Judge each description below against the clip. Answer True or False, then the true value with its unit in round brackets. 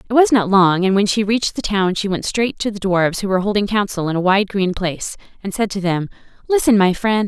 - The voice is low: False (200 Hz)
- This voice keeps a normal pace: False (265 wpm)